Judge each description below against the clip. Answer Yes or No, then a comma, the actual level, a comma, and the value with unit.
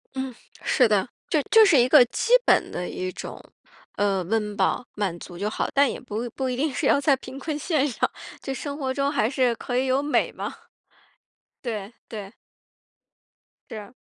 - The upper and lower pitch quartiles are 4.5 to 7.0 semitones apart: Yes, average, 4.9 semitones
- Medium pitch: No, very high, 250 Hz